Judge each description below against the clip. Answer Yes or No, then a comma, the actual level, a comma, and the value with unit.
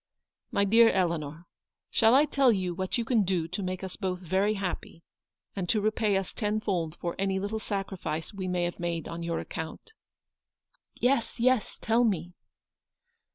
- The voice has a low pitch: No, high, 190 Hz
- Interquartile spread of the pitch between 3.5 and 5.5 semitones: Yes, average, 3.8 semitones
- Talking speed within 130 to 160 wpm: No, average, 180 wpm